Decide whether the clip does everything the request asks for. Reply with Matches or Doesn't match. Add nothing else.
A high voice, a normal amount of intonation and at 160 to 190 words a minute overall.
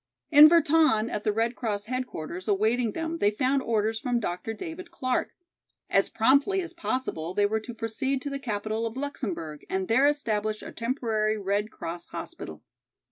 Matches